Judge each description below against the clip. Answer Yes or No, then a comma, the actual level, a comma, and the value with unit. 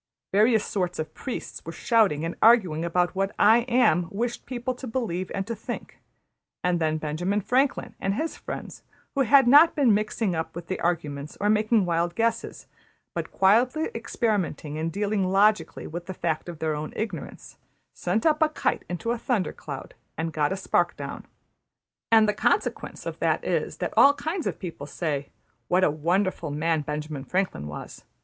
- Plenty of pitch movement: Yes, wide, 5.7 semitones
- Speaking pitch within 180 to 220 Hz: Yes, high, 190 Hz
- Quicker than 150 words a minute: Yes, average, 175 wpm